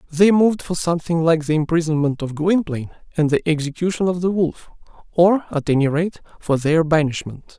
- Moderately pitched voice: Yes, medium, 165 Hz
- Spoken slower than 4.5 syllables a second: No, 5.6 syllables/s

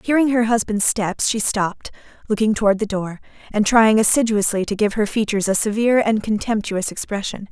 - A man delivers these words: No, female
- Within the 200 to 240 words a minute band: No, average, 175 wpm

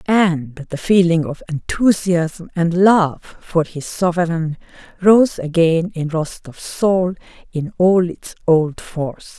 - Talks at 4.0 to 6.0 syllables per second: No, 3.4 syllables/s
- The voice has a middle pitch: Yes, medium, 170 Hz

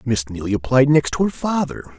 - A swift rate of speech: Yes, fast, 210 wpm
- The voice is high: No, low, 125 Hz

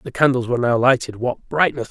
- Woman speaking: No, male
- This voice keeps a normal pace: Yes, average, 190 wpm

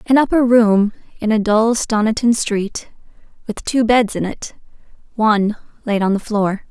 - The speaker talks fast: No, average, 150 wpm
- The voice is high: Yes, high, 220 Hz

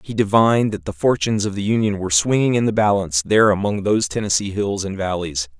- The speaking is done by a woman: No, male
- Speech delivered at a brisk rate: Yes, fast, 215 wpm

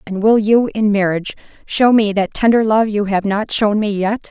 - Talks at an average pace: No, fast, 225 wpm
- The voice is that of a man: No, female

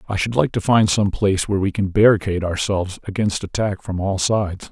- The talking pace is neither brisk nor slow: No, fast, 215 wpm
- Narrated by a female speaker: No, male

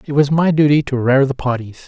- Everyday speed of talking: No, fast, 255 wpm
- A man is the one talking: Yes, male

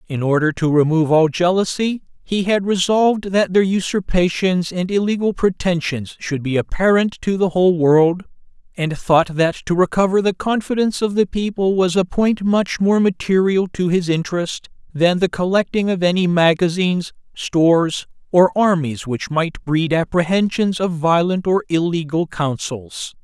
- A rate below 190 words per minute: Yes, average, 150 wpm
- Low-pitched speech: No, medium, 180 Hz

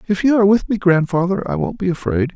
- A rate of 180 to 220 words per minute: No, fast, 255 wpm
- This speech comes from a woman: No, male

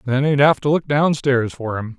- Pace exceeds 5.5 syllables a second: No, 4.9 syllables/s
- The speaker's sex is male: Yes, male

